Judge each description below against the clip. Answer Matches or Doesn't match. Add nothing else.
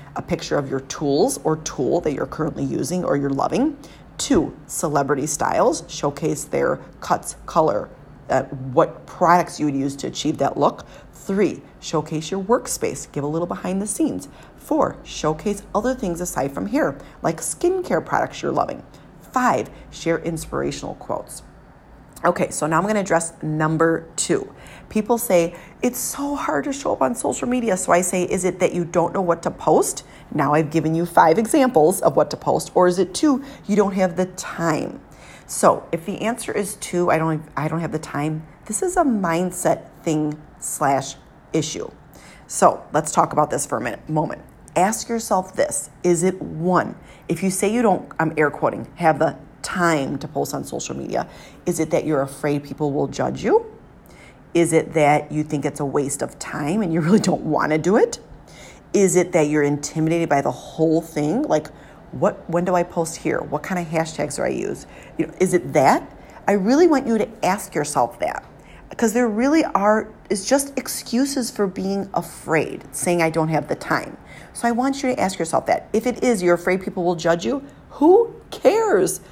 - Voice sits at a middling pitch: Matches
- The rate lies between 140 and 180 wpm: Doesn't match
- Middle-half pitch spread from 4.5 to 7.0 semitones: Matches